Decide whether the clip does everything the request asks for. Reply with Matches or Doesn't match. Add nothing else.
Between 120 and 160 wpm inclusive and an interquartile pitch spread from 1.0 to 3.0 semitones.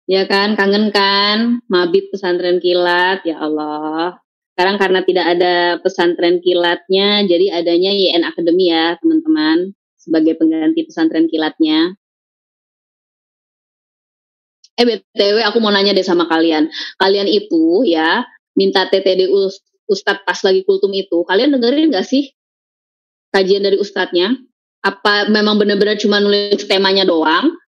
Doesn't match